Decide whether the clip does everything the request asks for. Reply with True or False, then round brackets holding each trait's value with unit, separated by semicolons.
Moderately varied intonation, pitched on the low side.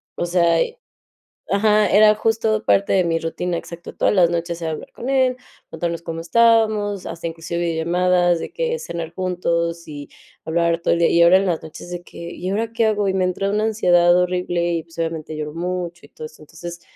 False (3.3 semitones; 175 Hz)